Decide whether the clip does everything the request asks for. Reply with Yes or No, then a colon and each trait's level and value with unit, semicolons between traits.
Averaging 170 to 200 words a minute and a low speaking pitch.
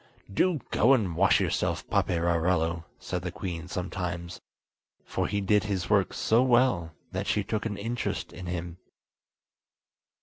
No: average, 140 wpm; very low, 95 Hz